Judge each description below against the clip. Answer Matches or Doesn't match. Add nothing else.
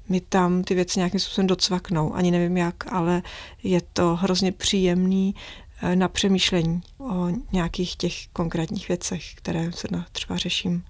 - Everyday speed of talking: Matches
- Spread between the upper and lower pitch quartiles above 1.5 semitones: Doesn't match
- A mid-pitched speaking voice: Matches